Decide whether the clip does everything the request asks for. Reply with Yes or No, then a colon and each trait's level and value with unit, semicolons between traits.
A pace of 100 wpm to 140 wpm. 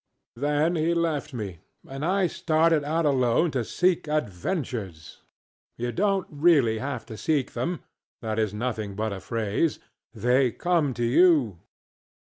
Yes: slow, 135 wpm